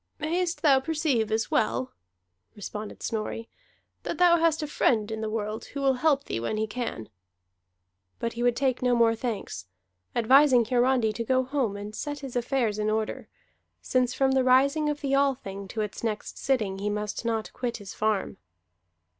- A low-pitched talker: No, high, 240 Hz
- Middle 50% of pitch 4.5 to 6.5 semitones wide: No, average, 4.1 semitones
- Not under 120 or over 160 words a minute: No, average, 180 wpm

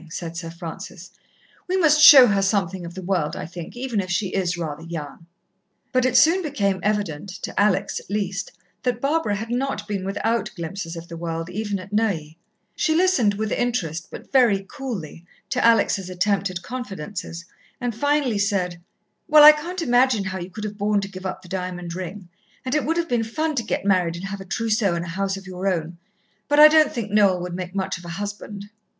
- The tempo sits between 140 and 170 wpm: No, fast, 205 wpm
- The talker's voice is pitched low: No, high, 200 Hz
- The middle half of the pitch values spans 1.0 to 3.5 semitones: No, average, 5.0 semitones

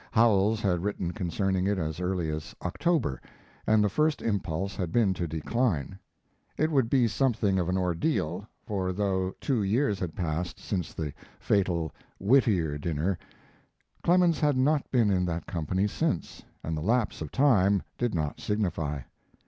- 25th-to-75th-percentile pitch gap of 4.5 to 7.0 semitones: Yes, average, 5.0 semitones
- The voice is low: Yes, very low, 95 Hz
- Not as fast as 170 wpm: Yes, average, 155 wpm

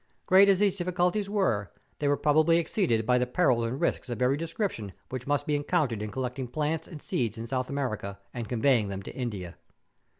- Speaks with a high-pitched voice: No, low, 130 Hz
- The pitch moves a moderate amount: No, wide, 6.2 semitones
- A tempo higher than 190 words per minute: Yes, fast, 205 wpm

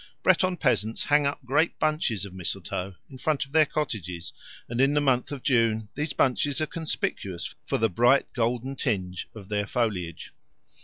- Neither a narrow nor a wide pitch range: No, wide, 5.9 semitones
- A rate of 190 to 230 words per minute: No, average, 170 wpm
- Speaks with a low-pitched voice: Yes, low, 125 Hz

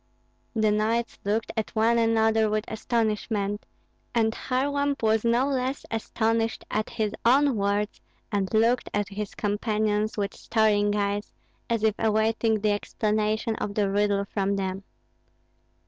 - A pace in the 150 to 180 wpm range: No, slow, 135 wpm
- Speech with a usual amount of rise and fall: No, narrow, 1.6 semitones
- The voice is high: Yes, high, 220 Hz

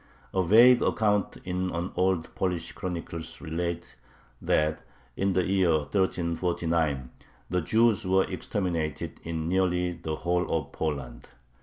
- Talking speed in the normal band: No, slow, 125 wpm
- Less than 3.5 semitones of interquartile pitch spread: Yes, narrow, 2.5 semitones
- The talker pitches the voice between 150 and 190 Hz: No, very low, 90 Hz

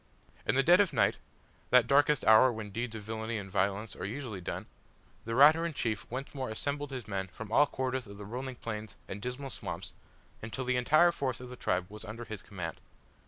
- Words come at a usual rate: No, fast, 210 wpm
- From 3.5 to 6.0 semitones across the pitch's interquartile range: Yes, average, 3.9 semitones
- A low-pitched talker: Yes, low, 120 Hz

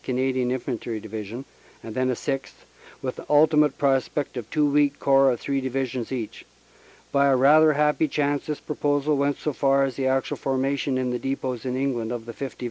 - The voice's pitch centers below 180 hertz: Yes, low, 135 Hz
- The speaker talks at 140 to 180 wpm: No, average, 200 wpm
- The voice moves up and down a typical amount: No, narrow, 2.1 semitones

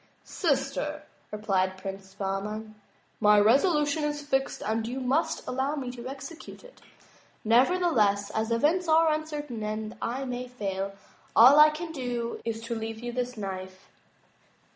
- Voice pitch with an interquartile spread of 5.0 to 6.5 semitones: Yes, wide, 5.6 semitones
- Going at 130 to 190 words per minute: Yes, average, 140 wpm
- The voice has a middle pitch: No, high, 245 Hz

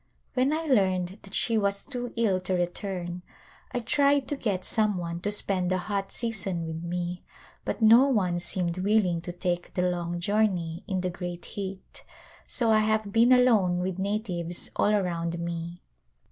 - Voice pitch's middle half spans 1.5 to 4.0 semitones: Yes, average, 3.6 semitones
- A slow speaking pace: No, average, 175 wpm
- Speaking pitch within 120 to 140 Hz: No, high, 190 Hz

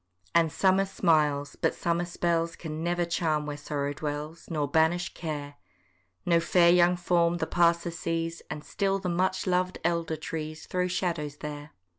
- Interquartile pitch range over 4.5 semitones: No, narrow, 2.4 semitones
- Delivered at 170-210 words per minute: No, average, 160 wpm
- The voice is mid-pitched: Yes, medium, 170 Hz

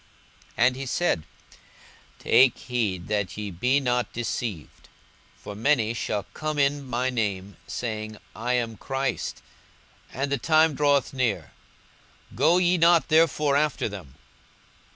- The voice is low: Yes, low, 125 Hz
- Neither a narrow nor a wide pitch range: Yes, average, 4.9 semitones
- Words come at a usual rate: No, slow, 130 wpm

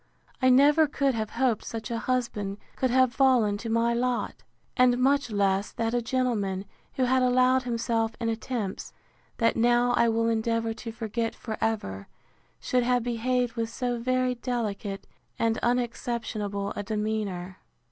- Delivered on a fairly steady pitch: Yes, narrow, 2.2 semitones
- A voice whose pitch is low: No, high, 235 Hz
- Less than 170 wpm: Yes, average, 155 wpm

